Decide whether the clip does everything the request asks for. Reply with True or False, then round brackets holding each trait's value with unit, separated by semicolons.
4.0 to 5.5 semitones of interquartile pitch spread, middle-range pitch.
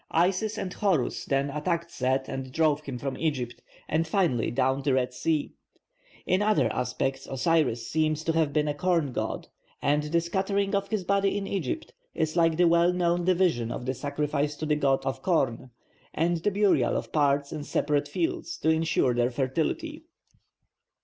True (4.7 semitones; 155 Hz)